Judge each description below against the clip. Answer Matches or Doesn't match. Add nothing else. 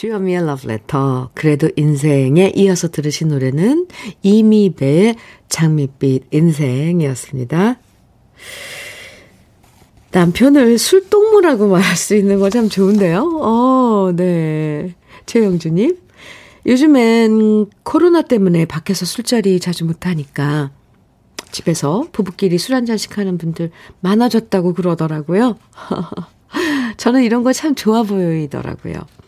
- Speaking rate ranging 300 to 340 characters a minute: Doesn't match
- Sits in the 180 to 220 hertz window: Matches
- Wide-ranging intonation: Matches